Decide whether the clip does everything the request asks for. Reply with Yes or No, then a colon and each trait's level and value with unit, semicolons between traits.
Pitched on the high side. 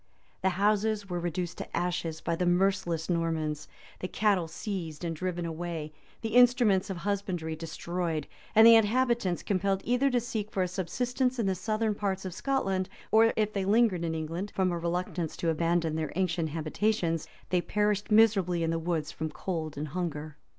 No: medium, 180 Hz